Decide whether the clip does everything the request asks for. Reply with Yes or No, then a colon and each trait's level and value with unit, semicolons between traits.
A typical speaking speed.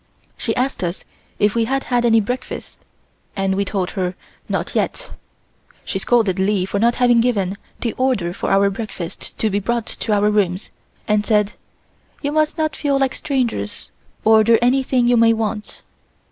Yes: average, 170 wpm